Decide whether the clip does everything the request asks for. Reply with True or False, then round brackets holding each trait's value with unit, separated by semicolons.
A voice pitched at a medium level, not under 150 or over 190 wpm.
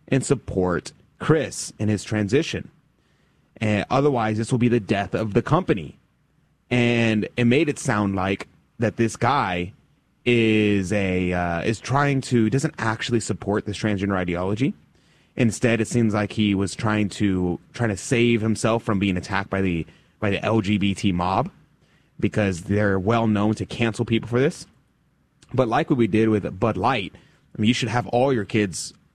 False (110 Hz; 170 wpm)